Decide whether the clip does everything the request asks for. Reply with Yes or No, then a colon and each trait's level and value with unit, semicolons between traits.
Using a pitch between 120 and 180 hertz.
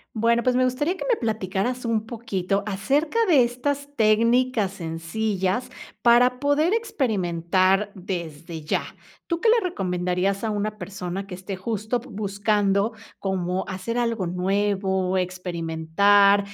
No: high, 205 Hz